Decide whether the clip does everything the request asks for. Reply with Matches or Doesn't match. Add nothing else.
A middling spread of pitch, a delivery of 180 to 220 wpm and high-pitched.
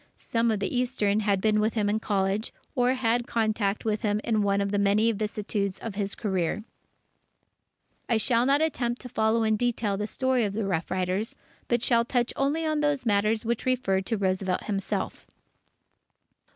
Matches